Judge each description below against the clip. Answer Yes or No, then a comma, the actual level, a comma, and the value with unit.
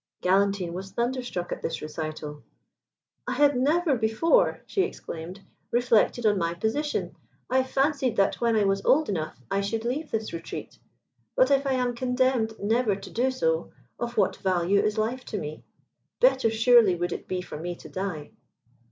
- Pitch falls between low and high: No, high, 220 Hz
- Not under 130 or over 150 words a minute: No, average, 170 wpm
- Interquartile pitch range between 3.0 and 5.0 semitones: No, wide, 5.4 semitones